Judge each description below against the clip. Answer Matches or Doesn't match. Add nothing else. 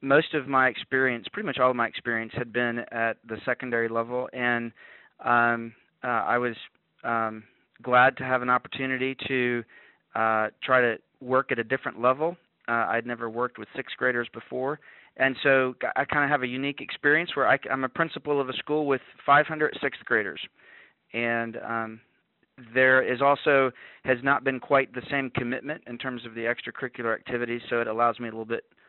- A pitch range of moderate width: Doesn't match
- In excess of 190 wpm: Doesn't match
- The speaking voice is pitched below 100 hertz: Doesn't match